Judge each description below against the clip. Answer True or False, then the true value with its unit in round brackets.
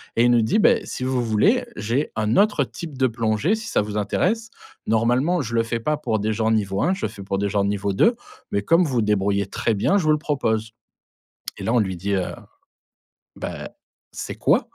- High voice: False (115 Hz)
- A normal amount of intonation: False (6.4 semitones)